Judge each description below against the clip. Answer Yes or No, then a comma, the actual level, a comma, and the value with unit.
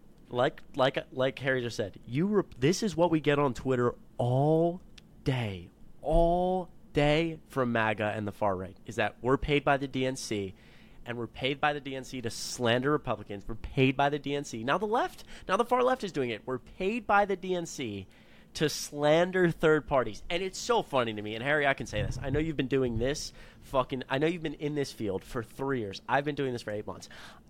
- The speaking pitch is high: No, low, 135 Hz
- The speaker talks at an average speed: No, fast, 220 wpm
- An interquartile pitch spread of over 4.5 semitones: Yes, average, 5.0 semitones